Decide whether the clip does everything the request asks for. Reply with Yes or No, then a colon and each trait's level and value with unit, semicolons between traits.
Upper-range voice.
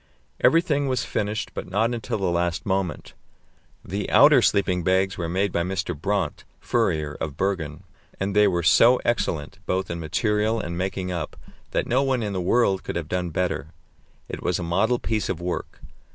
No: very low, 95 Hz